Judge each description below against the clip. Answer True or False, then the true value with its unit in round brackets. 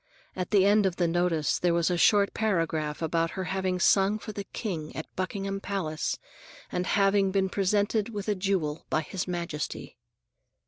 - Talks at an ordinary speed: True (175 wpm)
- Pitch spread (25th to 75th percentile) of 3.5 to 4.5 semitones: False (2.9 semitones)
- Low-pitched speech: False (190 Hz)